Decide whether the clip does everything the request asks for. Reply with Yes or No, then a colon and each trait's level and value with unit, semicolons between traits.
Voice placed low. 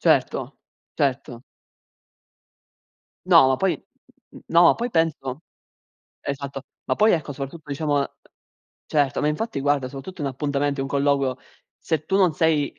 No: medium, 145 Hz